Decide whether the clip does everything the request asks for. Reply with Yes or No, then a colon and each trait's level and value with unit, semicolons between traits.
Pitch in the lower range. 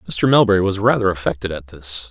Yes: very low, 95 Hz